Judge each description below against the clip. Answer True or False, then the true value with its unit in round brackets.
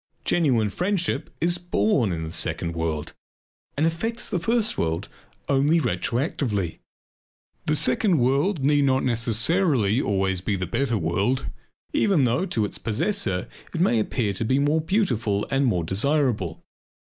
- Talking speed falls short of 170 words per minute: True (150 wpm)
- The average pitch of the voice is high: False (130 Hz)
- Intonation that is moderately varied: False (8.2 semitones)